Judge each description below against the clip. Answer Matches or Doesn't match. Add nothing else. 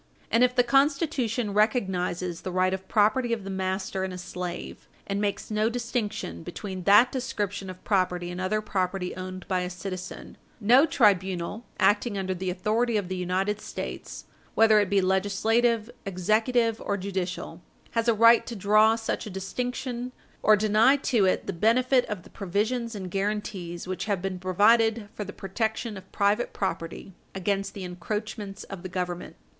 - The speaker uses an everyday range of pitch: Matches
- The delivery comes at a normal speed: Matches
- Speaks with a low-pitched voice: Doesn't match